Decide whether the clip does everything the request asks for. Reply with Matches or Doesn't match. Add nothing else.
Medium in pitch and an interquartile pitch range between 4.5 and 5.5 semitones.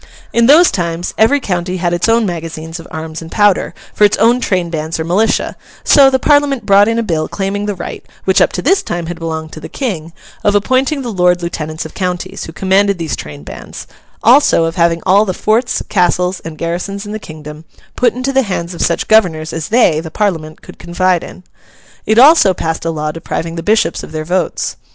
Matches